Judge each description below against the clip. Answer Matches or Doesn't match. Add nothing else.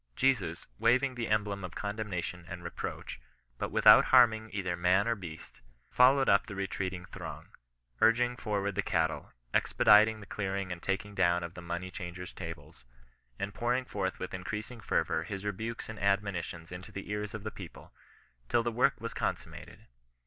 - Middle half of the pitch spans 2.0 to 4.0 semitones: Matches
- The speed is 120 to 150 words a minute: Doesn't match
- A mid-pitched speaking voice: Doesn't match